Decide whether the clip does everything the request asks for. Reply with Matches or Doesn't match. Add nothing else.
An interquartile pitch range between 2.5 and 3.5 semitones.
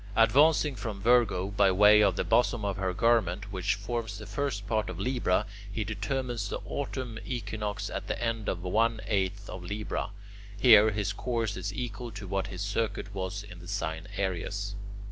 Matches